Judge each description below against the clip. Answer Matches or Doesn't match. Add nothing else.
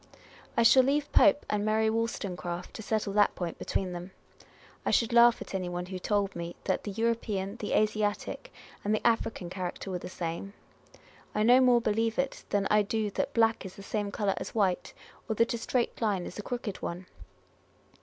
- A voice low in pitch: Doesn't match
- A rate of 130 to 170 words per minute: Doesn't match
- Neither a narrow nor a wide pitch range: Matches